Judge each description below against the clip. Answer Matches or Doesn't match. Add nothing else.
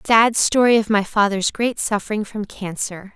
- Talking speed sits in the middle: Matches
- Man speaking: Doesn't match